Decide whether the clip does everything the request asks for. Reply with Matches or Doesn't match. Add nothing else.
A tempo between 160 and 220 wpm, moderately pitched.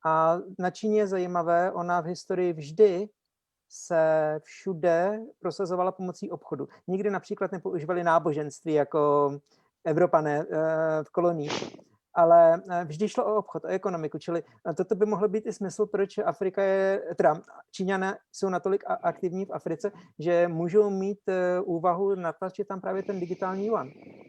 Doesn't match